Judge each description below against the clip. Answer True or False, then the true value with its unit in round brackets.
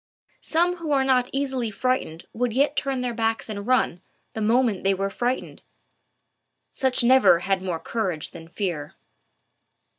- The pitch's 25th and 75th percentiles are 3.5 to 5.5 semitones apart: True (5.1 semitones)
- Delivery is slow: False (150 wpm)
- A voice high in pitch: True (235 Hz)